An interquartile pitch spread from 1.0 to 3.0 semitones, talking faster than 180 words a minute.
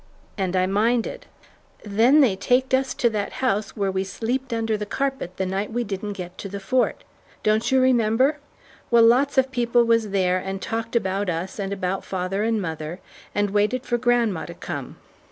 No: average, 4.0 semitones; average, 190 wpm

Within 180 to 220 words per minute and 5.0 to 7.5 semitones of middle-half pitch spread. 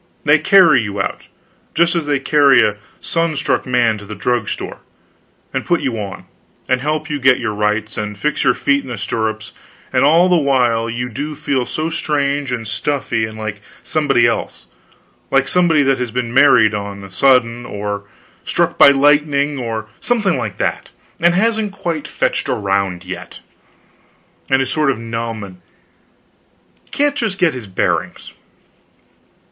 No: average, 165 wpm; wide, 5.5 semitones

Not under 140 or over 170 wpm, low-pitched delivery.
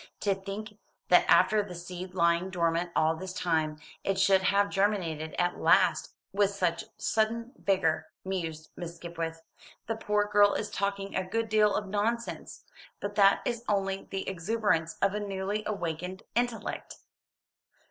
No: average, 150 wpm; high, 195 Hz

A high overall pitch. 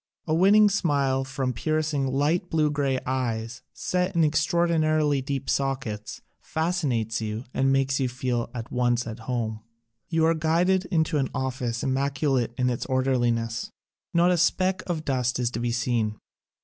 No: low, 135 Hz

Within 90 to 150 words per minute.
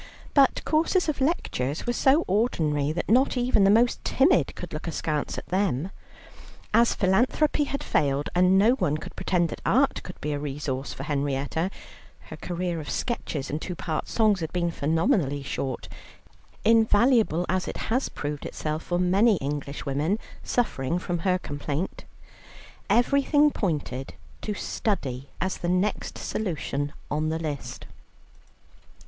Yes: average, 145 wpm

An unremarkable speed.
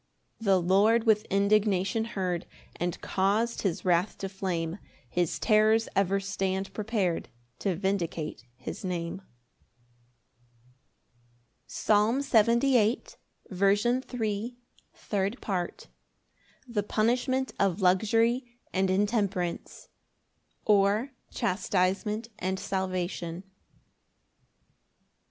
No: slow, 85 wpm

